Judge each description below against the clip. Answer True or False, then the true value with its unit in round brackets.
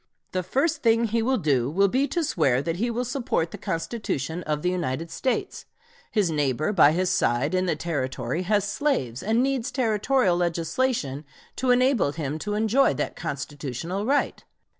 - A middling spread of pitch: False (7.8 semitones)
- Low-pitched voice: False (185 Hz)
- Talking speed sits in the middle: True (170 wpm)